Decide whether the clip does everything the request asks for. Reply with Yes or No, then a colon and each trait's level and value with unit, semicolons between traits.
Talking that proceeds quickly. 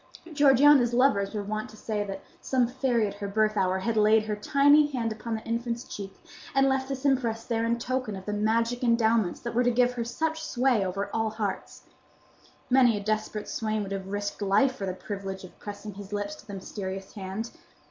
Yes: fast, 210 wpm